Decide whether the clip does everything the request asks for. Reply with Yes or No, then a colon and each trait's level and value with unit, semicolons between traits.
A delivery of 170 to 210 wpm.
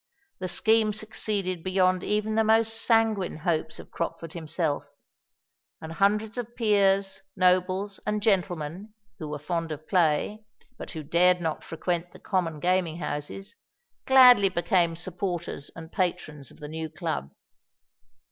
No: average, 140 wpm